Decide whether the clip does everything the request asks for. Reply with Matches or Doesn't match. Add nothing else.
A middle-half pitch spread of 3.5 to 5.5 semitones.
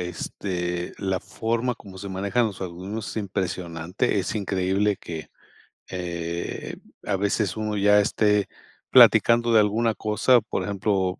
Doesn't match